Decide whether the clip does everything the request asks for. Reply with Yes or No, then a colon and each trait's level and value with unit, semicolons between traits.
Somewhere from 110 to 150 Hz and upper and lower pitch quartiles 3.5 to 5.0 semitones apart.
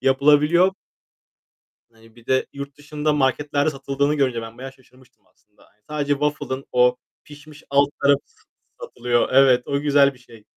No: medium, 140 Hz; narrow, 2.5 semitones